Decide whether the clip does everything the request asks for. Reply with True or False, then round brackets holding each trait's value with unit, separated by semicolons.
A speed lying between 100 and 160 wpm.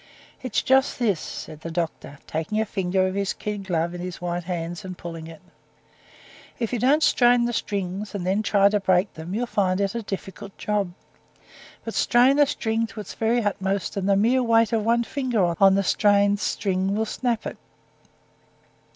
False (190 wpm)